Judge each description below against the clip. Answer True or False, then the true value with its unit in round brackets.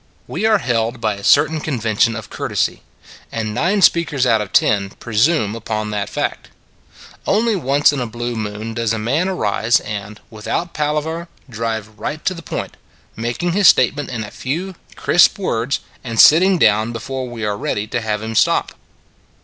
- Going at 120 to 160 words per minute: False (175 wpm)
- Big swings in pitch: True (5.9 semitones)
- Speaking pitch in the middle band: False (120 Hz)